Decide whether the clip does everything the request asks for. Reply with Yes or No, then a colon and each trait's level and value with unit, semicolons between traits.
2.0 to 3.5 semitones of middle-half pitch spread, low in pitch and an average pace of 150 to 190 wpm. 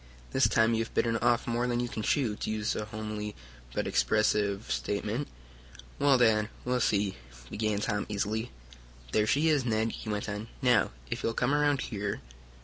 Yes: narrow, 2.6 semitones; low, 110 Hz; average, 180 wpm